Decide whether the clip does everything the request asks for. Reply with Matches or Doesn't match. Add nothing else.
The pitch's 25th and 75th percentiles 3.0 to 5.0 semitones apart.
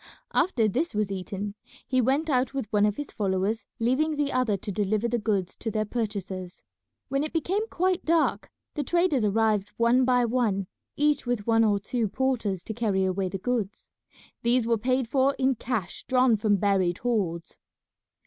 Matches